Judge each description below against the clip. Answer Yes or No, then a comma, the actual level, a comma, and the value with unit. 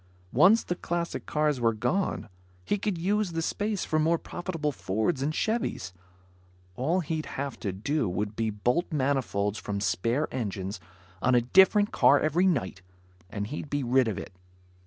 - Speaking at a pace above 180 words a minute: No, average, 165 wpm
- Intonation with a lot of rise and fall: Yes, wide, 7.7 semitones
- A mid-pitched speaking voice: Yes, medium, 145 Hz